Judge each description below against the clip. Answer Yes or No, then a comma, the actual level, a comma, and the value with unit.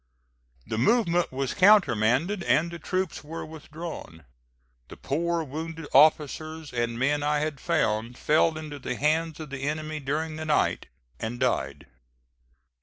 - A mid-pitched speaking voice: Yes, medium, 155 Hz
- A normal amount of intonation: Yes, average, 3.4 semitones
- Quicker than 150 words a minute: No, average, 140 wpm